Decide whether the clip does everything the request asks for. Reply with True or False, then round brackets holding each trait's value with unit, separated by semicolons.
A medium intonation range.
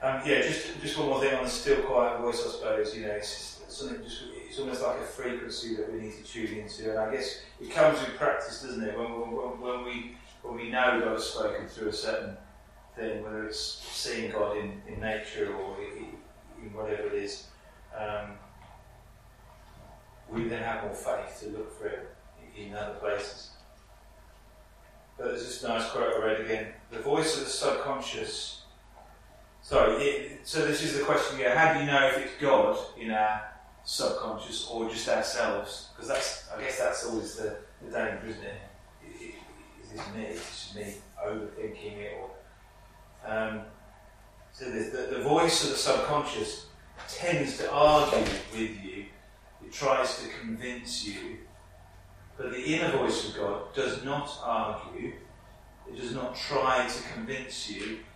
True (4.2 semitones)